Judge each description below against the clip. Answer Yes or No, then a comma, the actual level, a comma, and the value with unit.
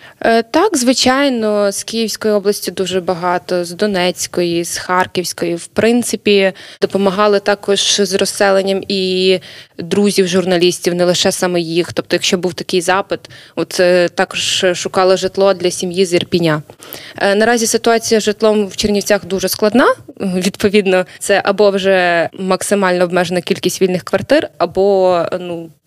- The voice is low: No, high, 190 Hz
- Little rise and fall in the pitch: Yes, narrow, 2.2 semitones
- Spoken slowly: No, average, 130 wpm